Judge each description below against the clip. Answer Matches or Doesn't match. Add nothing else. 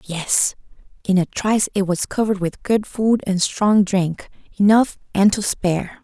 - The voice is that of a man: Doesn't match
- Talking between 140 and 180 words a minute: Matches